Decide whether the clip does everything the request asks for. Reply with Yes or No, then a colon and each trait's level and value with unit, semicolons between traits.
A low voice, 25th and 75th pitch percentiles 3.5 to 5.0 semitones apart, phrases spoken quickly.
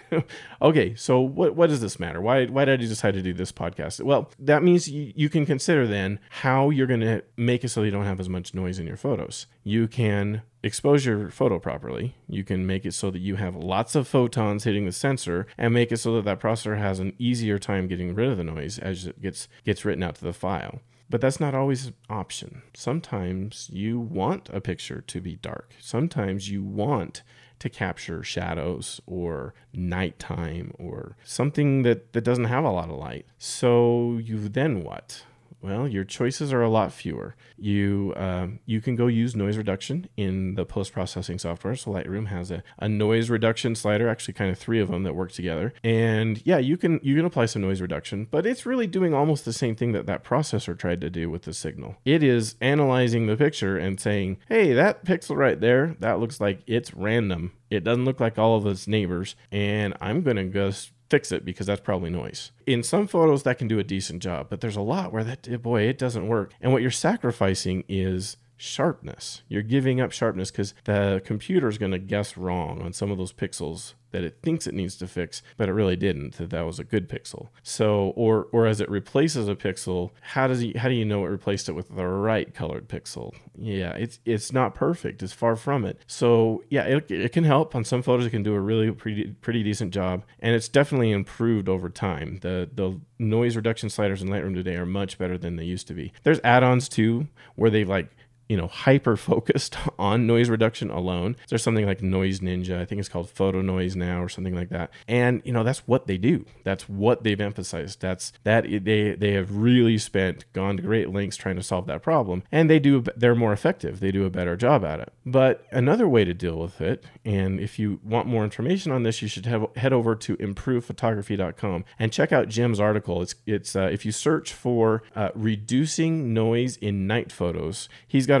Yes: low, 110 Hz; average, 4.2 semitones; fast, 215 wpm